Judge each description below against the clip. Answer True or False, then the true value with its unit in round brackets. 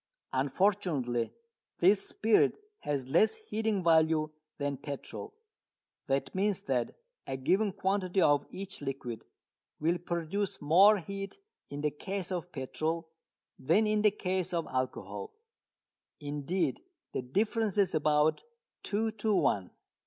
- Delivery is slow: True (125 wpm)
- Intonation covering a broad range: True (5.7 semitones)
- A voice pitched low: False (175 Hz)